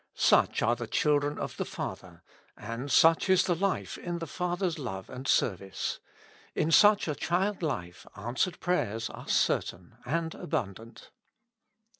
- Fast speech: No, average, 140 wpm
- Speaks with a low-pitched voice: No, medium, 150 Hz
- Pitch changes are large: Yes, wide, 7.2 semitones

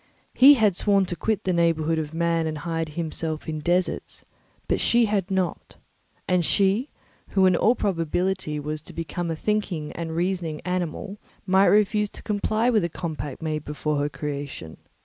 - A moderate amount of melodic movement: Yes, average, 3.9 semitones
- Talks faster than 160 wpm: Yes, average, 170 wpm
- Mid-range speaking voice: Yes, medium, 170 Hz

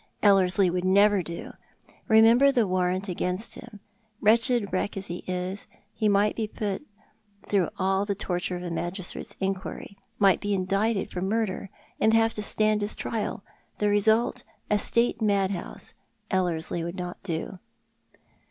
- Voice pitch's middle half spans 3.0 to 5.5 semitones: No, narrow, 2.6 semitones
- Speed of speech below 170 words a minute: Yes, average, 160 wpm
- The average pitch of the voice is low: No, high, 195 Hz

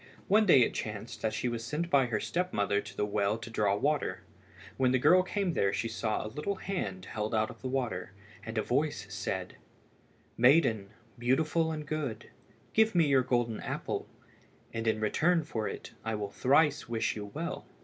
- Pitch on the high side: No, low, 120 Hz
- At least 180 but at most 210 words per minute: Yes, average, 190 wpm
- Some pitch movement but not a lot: No, wide, 6.2 semitones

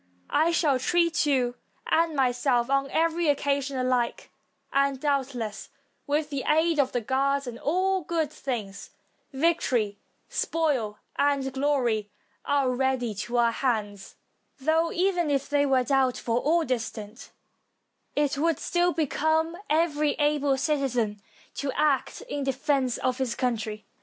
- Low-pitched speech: No, very high, 275 Hz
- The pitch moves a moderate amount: Yes, average, 3.5 semitones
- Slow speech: Yes, slow, 130 wpm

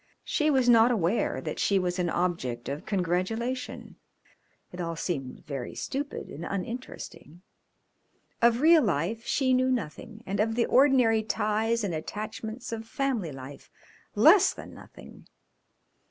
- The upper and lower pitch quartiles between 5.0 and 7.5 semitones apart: Yes, wide, 5.6 semitones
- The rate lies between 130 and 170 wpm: Yes, average, 140 wpm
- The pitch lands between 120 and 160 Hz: No, high, 215 Hz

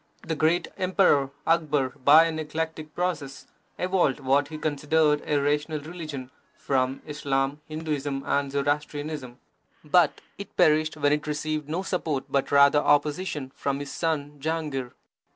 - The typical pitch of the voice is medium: Yes, medium, 150 Hz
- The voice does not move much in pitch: Yes, narrow, 1.9 semitones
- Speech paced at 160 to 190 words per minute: No, slow, 135 wpm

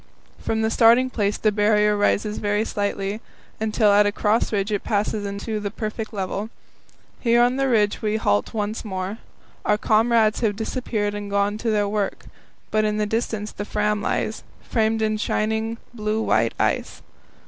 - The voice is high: Yes, high, 215 Hz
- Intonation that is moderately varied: No, narrow, 1.3 semitones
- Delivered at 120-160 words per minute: No, average, 170 wpm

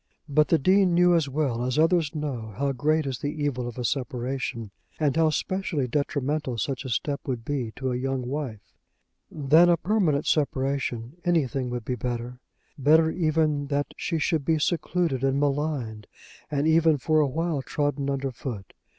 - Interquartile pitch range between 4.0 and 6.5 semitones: No, average, 3.5 semitones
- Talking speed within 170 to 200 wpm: Yes, average, 175 wpm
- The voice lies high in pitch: No, medium, 140 Hz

